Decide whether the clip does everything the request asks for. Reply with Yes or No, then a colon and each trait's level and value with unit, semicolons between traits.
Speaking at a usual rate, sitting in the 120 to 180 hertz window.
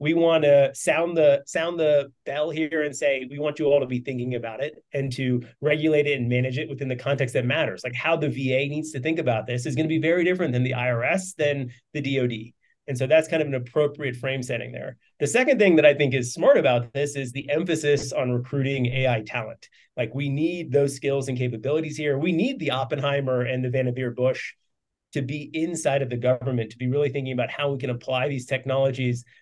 No: fast, 230 wpm; medium, 140 Hz